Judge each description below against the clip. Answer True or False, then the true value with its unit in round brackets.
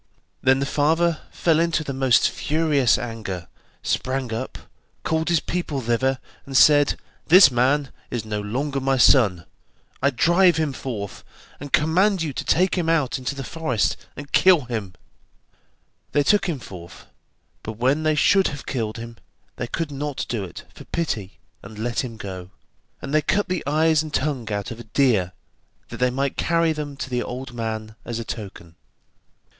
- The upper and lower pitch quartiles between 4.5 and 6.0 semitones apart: True (5.2 semitones)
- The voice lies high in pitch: False (135 Hz)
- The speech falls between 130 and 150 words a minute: False (175 wpm)